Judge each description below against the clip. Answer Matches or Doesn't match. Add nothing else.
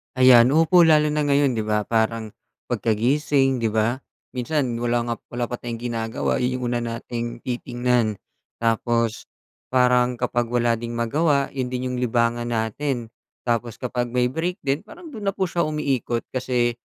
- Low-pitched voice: Matches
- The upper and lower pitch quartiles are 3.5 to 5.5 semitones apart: Doesn't match